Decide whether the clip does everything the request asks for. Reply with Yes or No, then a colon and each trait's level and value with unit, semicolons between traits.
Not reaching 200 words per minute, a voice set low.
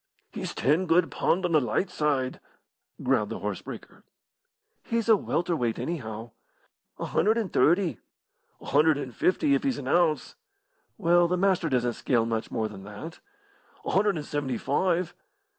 No: average, 165 wpm; medium, 160 Hz